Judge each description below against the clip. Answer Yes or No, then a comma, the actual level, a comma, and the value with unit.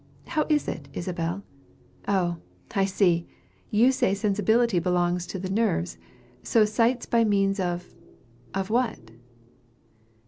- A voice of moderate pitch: No, high, 195 Hz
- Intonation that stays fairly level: No, average, 4.2 semitones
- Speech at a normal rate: No, slow, 125 wpm